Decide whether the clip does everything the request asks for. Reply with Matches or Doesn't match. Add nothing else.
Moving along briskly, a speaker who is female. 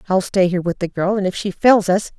Matches